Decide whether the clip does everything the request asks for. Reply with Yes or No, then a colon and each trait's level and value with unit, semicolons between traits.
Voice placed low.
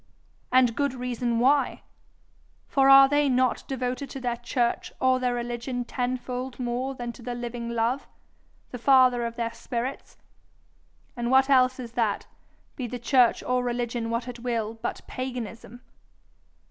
No: high, 245 Hz